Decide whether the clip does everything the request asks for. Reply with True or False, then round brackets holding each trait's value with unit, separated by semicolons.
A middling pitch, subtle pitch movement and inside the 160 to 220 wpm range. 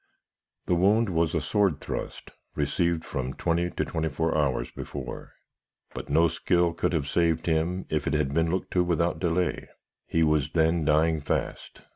False (80 Hz; 2.1 semitones; 170 wpm)